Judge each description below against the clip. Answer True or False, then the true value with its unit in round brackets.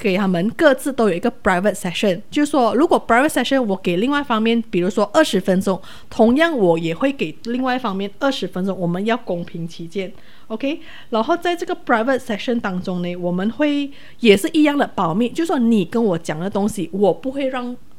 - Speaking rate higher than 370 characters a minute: True (420 characters per minute)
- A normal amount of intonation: False (5.9 semitones)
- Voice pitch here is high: True (225 Hz)